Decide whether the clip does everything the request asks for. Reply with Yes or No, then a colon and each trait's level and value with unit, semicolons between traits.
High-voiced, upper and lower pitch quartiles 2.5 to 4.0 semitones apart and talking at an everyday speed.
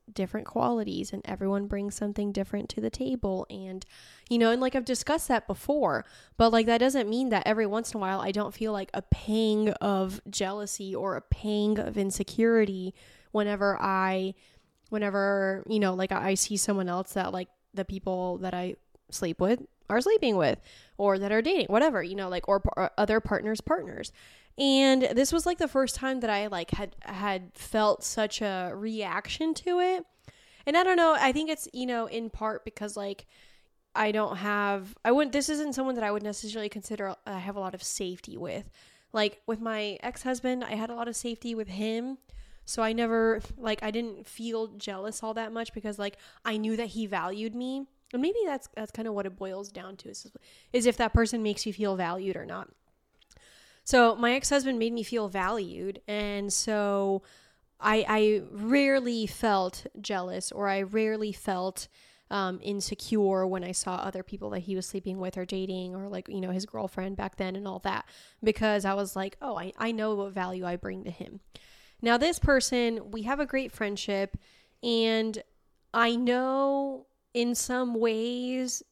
Yes: high, 215 Hz; average, 3.2 semitones; average, 190 wpm